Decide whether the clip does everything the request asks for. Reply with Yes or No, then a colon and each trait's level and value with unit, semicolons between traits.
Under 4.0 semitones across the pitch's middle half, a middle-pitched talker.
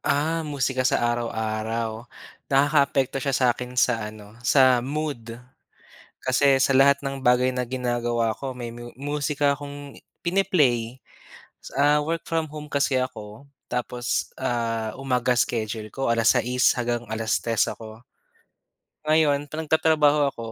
No: average, 3.5 semitones; low, 130 Hz